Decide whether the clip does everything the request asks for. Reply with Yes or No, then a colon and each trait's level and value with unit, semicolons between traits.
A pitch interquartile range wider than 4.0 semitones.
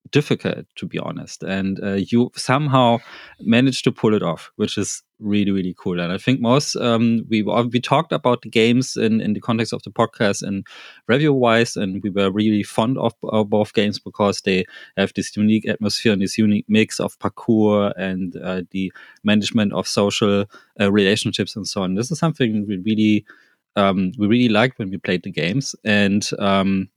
No: average, 2.9 semitones